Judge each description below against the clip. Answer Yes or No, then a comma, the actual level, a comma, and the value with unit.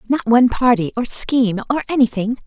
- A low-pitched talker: No, high, 240 Hz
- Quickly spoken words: No, average, 170 wpm